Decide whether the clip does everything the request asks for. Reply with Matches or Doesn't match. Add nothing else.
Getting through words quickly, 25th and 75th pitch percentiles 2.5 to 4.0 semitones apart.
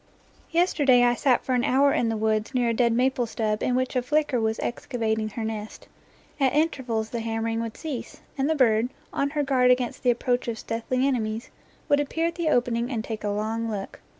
Matches